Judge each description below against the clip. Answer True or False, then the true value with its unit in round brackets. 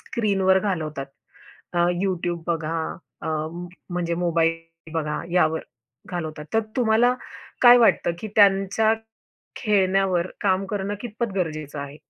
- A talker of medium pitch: True (180 Hz)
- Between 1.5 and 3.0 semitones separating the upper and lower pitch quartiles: False (3.6 semitones)